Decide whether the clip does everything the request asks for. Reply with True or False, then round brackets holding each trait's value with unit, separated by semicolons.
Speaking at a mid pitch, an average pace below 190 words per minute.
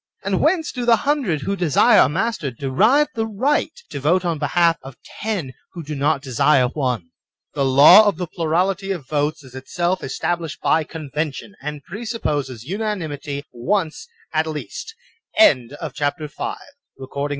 True (160 Hz; 160 wpm)